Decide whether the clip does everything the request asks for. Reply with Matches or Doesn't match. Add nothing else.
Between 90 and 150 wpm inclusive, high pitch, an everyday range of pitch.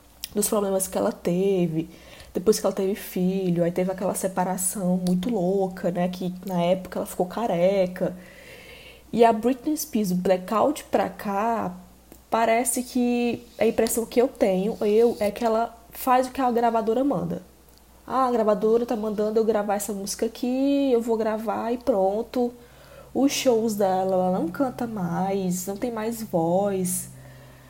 Doesn't match